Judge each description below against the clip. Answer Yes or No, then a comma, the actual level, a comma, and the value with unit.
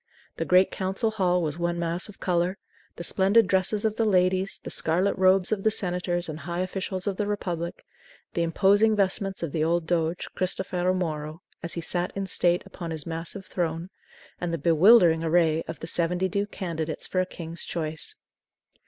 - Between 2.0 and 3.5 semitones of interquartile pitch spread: Yes, narrow, 2.4 semitones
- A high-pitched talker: No, medium, 180 Hz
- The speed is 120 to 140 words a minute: No, average, 185 wpm